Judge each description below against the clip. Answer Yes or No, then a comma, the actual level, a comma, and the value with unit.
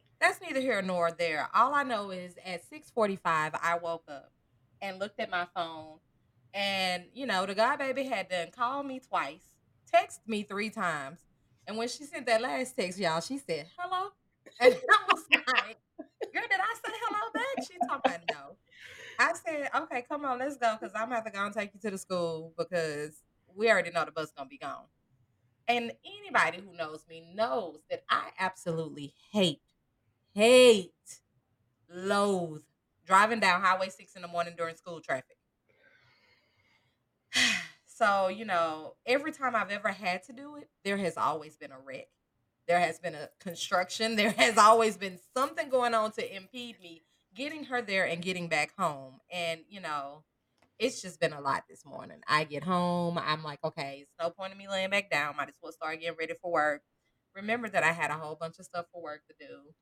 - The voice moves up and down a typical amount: No, wide, 6.5 semitones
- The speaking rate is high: No, average, 195 wpm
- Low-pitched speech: No, medium, 185 Hz